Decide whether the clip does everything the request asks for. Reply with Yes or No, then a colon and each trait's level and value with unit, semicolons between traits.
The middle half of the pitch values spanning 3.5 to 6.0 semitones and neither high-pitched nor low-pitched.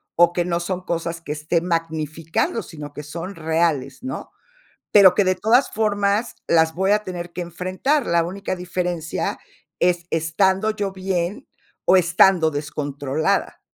No: average, 2.8 semitones; medium, 175 Hz